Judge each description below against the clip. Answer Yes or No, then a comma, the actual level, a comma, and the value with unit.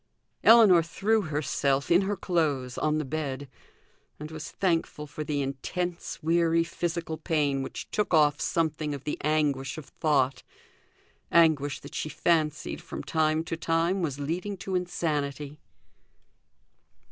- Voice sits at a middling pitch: Yes, medium, 155 Hz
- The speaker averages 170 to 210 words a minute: No, slow, 135 wpm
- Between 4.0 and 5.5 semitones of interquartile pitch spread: No, average, 2.8 semitones